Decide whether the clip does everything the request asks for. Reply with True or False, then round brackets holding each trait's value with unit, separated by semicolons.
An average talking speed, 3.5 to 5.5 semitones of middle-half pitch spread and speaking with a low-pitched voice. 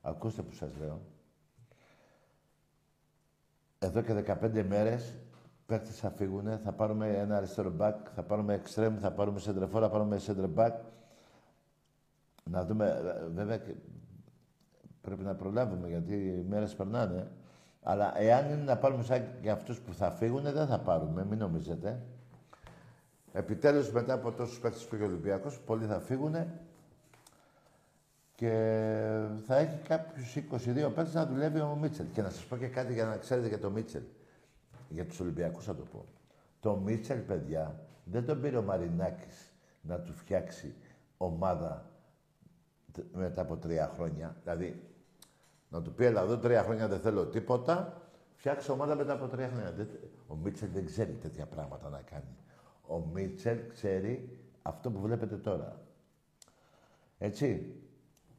True (145 wpm; 4.3 semitones; 110 Hz)